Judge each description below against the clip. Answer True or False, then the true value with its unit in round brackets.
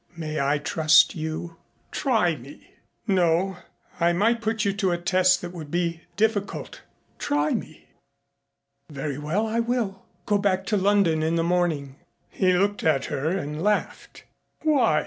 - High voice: False (175 Hz)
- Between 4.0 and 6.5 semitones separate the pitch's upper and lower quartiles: True (4.4 semitones)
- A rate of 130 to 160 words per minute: True (150 wpm)